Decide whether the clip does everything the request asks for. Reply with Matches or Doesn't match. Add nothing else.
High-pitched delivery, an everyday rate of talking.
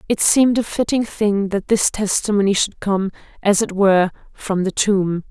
Matches